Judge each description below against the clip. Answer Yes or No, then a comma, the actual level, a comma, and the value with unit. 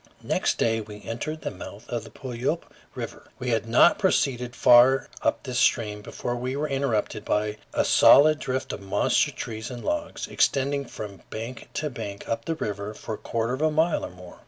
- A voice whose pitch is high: No, low, 120 Hz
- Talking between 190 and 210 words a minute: Yes, average, 195 wpm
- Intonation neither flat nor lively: Yes, average, 4.2 semitones